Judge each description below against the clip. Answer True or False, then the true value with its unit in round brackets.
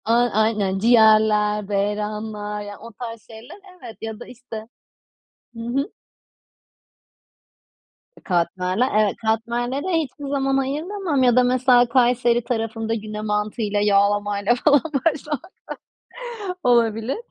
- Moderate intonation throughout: True (3.1 semitones)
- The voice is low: False (225 Hz)